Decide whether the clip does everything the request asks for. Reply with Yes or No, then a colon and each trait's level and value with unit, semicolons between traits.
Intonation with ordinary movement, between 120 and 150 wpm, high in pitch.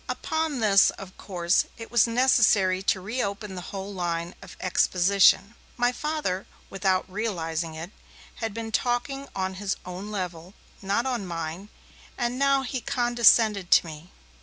Yes: average, 4.7 semitones; average, 145 wpm; high, 200 Hz